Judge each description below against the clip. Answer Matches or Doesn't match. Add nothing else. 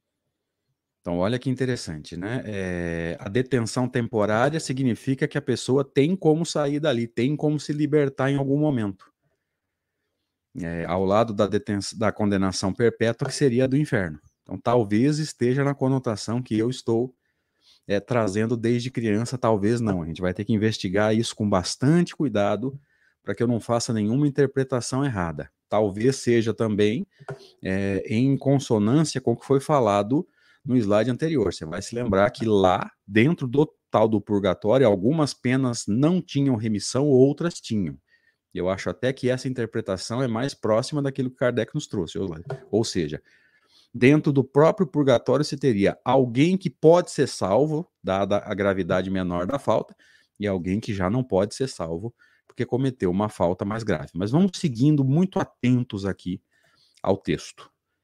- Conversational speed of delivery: Matches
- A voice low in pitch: Matches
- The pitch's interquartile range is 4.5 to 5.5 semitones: Matches